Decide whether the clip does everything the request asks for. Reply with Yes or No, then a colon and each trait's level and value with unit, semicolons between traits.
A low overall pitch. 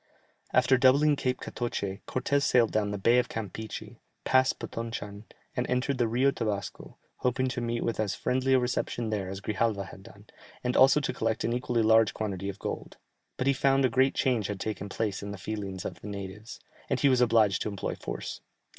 Yes: low, 115 Hz